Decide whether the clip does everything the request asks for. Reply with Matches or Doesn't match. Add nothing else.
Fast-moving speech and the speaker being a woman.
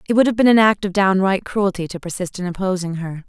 Matches